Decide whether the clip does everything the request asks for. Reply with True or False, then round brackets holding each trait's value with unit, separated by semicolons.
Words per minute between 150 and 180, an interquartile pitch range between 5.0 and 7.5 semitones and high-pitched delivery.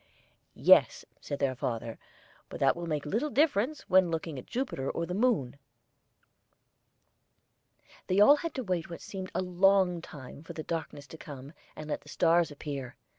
False (170 wpm; 5.3 semitones; 170 Hz)